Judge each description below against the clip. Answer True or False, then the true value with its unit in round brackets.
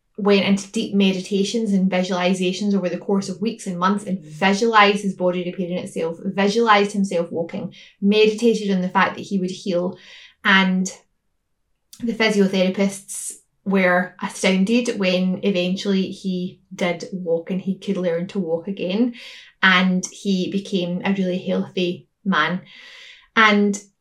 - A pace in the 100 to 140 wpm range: True (135 wpm)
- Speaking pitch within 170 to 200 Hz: True (190 Hz)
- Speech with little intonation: True (1.9 semitones)